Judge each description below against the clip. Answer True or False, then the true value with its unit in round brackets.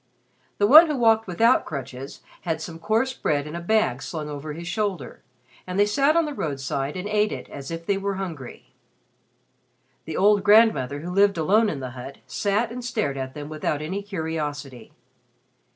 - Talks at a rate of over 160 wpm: True (185 wpm)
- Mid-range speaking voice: True (175 Hz)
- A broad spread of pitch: True (6.3 semitones)